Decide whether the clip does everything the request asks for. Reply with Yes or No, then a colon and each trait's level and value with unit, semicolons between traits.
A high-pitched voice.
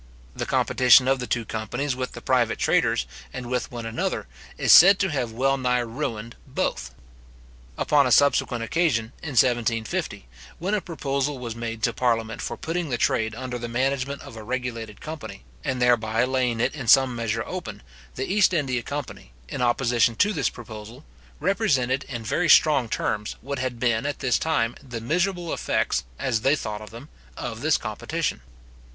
No: low, 125 Hz